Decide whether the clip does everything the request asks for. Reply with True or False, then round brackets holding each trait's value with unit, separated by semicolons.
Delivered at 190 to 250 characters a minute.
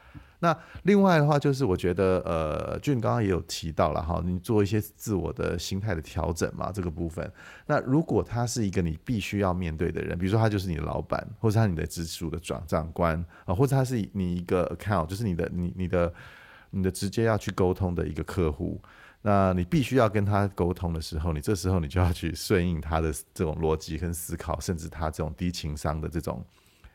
False (335 characters per minute)